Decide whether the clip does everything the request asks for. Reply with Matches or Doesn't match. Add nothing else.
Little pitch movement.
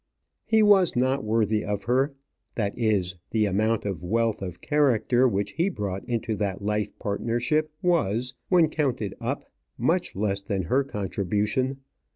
Doesn't match